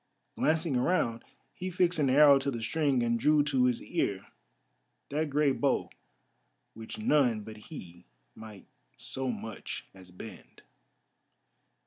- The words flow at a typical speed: No, slow, 130 wpm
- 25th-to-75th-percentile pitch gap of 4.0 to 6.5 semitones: Yes, average, 5.1 semitones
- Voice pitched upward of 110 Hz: Yes, low, 135 Hz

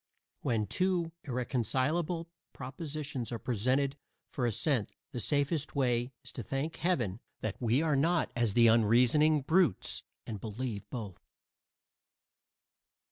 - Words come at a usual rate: No, slow, 120 wpm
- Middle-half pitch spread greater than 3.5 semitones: Yes, average, 4.7 semitones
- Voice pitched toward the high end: No, low, 130 Hz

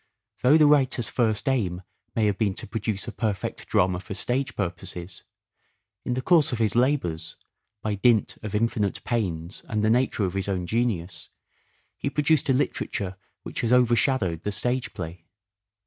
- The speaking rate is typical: Yes, average, 165 wpm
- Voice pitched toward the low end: Yes, low, 110 Hz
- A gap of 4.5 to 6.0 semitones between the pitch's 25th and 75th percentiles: Yes, average, 5.0 semitones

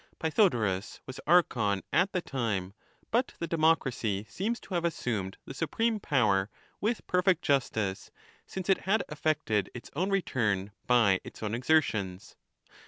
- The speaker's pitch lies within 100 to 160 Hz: Yes, low, 135 Hz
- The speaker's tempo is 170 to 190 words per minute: No, average, 145 wpm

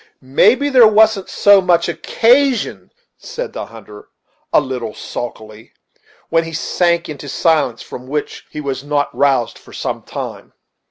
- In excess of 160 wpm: No, average, 150 wpm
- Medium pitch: Yes, medium, 160 Hz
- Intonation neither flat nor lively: No, wide, 8.2 semitones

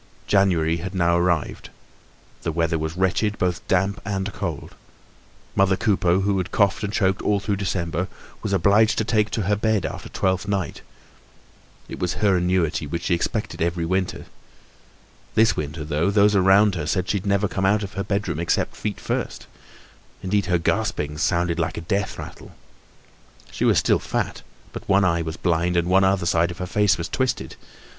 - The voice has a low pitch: Yes, very low, 95 Hz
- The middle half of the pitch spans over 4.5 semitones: No, average, 2.8 semitones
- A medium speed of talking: Yes, average, 180 wpm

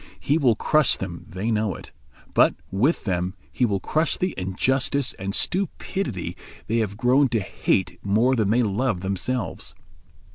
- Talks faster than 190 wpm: No, average, 155 wpm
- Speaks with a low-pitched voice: Yes, low, 115 Hz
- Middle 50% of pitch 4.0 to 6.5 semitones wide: Yes, wide, 5.4 semitones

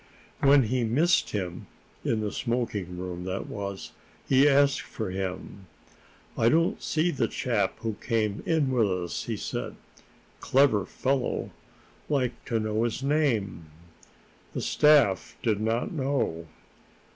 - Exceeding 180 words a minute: No, slow, 135 wpm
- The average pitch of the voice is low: Yes, low, 115 Hz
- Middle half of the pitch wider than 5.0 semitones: Yes, wide, 5.6 semitones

